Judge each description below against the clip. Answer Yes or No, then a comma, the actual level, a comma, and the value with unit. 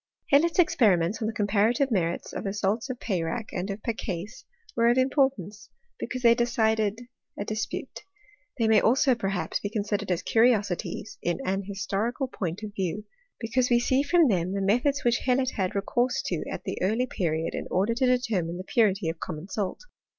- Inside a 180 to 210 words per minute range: Yes, average, 185 wpm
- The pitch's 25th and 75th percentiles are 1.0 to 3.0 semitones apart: No, average, 4.2 semitones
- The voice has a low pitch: No, high, 215 Hz